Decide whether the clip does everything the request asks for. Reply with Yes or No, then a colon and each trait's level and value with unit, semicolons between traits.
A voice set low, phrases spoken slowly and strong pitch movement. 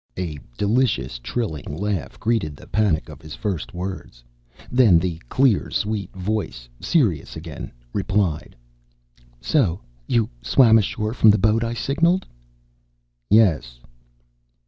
Yes: low, 100 Hz; slow, 120 wpm; wide, 5.9 semitones